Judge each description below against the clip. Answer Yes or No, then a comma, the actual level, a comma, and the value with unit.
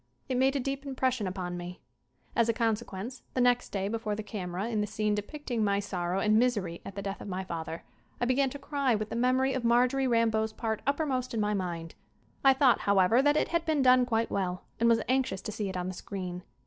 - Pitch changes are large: No, average, 4.7 semitones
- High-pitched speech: Yes, high, 225 Hz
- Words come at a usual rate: No, fast, 235 wpm